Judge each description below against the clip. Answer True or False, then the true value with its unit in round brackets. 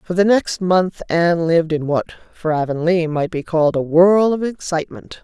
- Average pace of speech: True (195 wpm)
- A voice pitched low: False (170 Hz)